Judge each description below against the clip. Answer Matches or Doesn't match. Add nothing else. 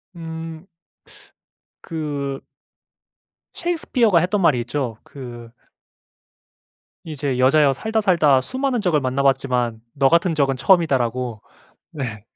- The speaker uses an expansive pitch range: Doesn't match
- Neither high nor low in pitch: Matches